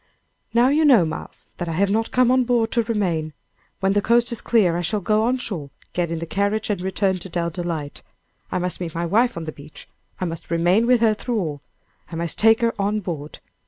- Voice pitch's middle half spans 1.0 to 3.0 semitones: No, average, 5.2 semitones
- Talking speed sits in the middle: No, fast, 230 wpm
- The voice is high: Yes, high, 195 Hz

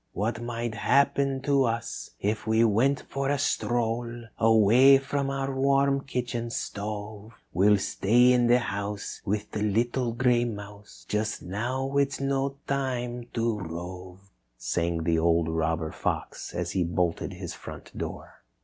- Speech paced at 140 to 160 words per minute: Yes, average, 150 wpm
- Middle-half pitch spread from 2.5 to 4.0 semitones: No, average, 4.5 semitones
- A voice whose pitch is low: Yes, low, 115 Hz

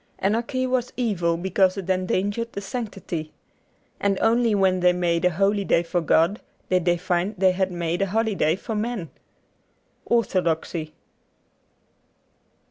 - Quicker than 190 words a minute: No, average, 140 wpm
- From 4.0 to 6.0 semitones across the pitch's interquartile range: No, average, 3.3 semitones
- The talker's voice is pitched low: No, high, 190 Hz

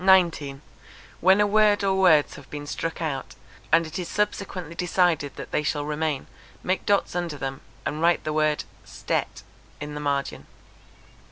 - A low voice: No, medium, 160 Hz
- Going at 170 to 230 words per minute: No, average, 160 wpm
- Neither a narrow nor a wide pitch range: Yes, average, 3.9 semitones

